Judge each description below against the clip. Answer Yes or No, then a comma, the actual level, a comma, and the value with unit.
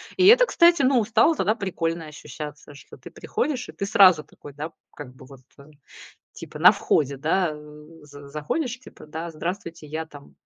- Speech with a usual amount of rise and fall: No, wide, 7.0 semitones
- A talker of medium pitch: Yes, medium, 165 Hz